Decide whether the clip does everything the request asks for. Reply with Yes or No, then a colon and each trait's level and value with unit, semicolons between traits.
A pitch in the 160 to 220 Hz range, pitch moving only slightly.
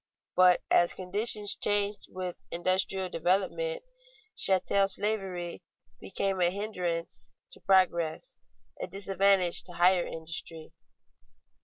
Yes: medium, 185 Hz; narrow, 2.3 semitones